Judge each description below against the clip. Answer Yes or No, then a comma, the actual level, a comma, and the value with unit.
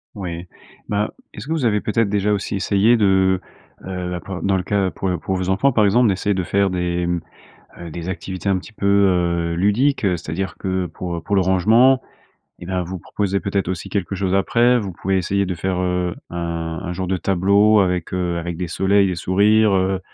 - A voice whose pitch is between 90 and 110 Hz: Yes, very low, 95 Hz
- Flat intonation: Yes, narrow, 2.1 semitones